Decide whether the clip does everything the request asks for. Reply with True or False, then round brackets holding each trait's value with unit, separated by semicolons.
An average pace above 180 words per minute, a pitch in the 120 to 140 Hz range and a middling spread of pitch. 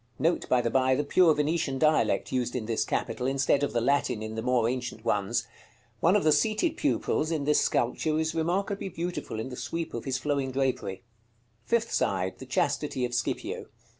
True (195 wpm; 135 Hz; 4.8 semitones)